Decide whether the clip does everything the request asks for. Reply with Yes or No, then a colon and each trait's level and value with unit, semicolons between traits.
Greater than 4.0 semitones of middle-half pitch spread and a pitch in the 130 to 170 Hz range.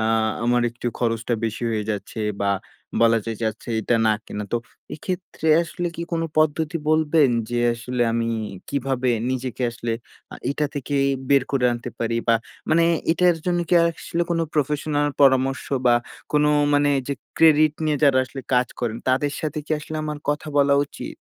Yes: average, 4.4 semitones; medium, 140 Hz